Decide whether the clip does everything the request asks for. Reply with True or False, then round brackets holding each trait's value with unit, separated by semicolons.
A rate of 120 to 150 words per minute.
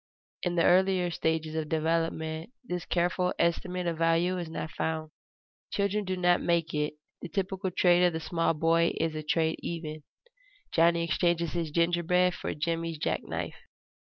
False (160 wpm)